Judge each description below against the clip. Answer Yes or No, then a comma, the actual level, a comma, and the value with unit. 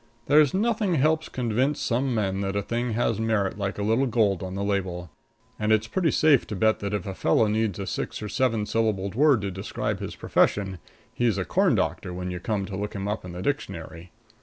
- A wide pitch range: No, average, 3.7 semitones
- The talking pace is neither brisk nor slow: No, fast, 220 wpm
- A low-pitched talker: Yes, low, 105 Hz